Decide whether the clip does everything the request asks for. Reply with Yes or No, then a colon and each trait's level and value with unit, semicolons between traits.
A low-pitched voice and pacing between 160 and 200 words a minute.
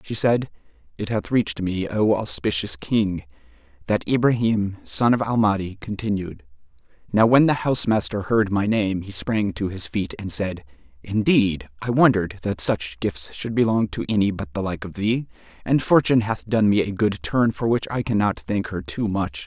Yes: low, 105 Hz; average, 190 wpm